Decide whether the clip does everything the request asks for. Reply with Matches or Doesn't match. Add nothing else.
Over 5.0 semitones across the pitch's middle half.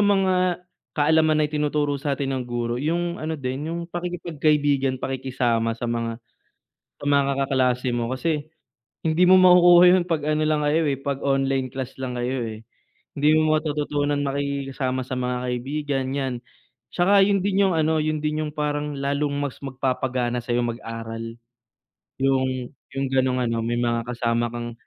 Doesn't match